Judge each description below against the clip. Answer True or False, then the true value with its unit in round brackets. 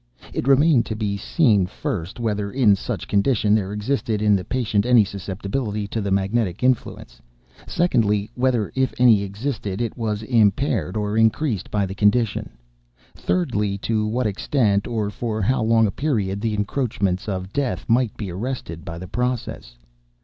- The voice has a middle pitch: False (105 Hz)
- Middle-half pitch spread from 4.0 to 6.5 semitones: False (3.3 semitones)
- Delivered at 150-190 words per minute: True (160 wpm)